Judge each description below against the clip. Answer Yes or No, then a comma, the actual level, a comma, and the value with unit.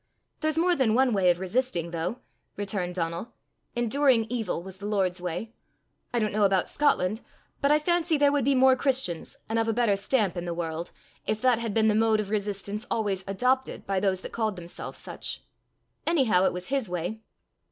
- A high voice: Yes, high, 215 Hz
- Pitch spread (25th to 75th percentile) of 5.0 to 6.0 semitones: Yes, wide, 5.4 semitones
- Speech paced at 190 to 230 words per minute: Yes, average, 195 wpm